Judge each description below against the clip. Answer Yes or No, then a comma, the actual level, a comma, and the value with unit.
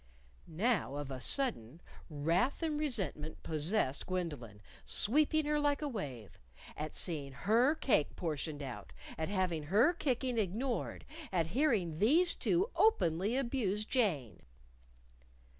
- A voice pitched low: No, high, 190 Hz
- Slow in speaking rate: Yes, slow, 125 wpm